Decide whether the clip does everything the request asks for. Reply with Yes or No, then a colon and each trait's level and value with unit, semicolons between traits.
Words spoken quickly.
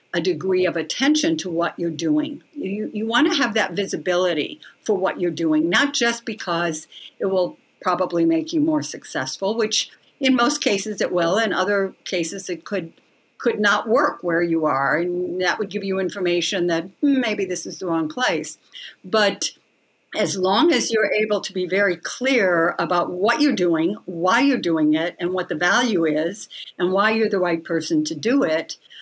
No: average, 190 wpm